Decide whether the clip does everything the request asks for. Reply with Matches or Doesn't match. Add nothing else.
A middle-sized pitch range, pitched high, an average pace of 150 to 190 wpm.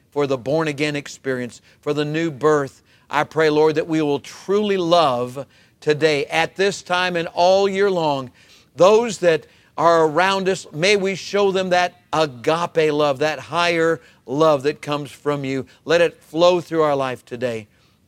Doesn't match